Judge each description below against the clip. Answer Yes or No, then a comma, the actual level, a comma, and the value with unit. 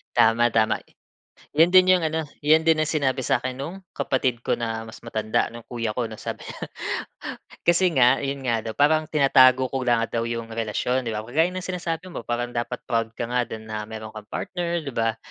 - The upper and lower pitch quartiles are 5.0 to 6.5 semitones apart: Yes, average, 5.3 semitones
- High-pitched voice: No, low, 125 Hz